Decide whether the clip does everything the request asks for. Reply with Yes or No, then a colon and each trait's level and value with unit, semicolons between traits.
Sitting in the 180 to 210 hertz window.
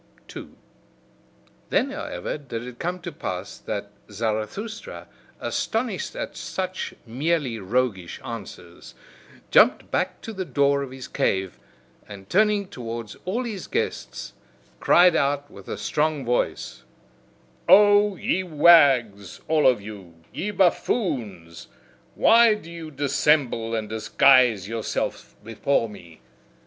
No: medium, 140 Hz